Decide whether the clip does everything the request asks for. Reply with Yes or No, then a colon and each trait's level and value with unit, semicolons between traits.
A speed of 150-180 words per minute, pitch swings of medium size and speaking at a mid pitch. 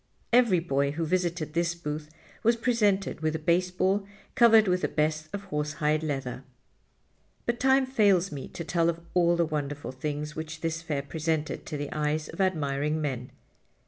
Yes: average, 170 wpm; average, 3.5 semitones; medium, 160 Hz